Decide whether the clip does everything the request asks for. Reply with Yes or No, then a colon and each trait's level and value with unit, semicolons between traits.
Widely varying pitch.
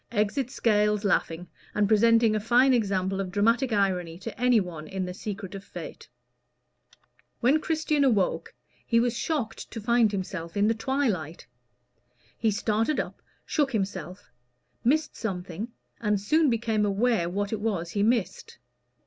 No: average, 3.6 semitones